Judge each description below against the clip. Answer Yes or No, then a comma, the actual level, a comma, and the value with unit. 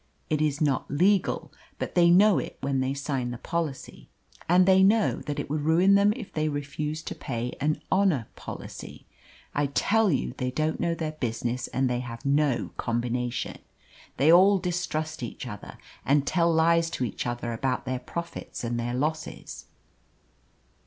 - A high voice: No, medium, 150 Hz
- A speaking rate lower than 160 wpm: No, average, 170 wpm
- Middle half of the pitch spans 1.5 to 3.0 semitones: No, average, 5.0 semitones